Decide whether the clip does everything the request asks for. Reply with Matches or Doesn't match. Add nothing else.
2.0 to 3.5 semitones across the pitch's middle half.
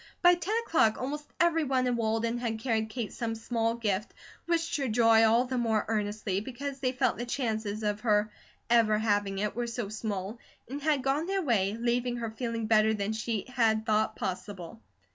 Matches